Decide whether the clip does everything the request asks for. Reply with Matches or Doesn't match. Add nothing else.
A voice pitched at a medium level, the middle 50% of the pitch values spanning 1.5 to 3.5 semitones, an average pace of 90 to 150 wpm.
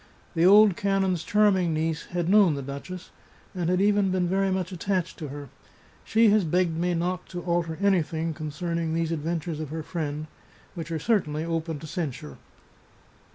Doesn't match